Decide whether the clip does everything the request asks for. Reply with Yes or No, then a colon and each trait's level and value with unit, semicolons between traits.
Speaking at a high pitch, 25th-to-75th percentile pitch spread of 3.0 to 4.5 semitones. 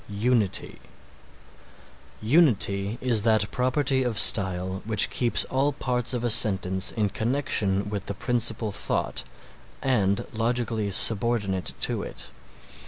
No: low, 110 Hz; average, 3.6 semitones